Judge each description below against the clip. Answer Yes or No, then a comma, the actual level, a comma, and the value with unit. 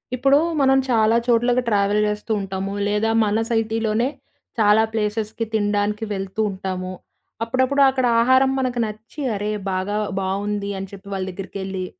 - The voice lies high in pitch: Yes, high, 210 Hz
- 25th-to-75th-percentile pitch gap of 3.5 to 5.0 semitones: No, average, 2.7 semitones